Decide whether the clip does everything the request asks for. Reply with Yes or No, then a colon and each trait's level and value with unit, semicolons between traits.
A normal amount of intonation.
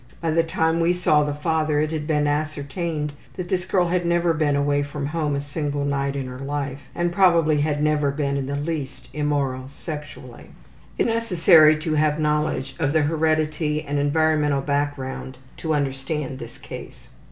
No: narrow, 2.0 semitones